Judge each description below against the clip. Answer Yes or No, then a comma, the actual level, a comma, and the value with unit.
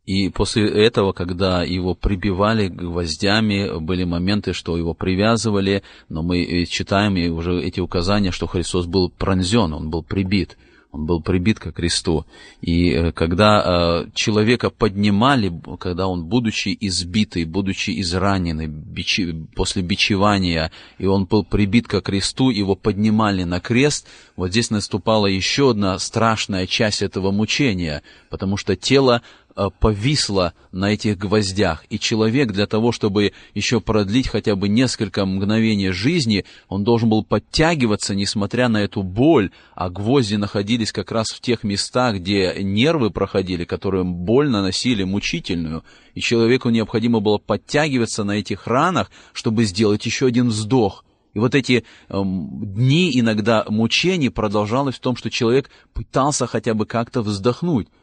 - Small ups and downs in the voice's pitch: No, average, 3.5 semitones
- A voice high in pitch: No, low, 100 Hz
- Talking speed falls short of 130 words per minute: No, average, 140 wpm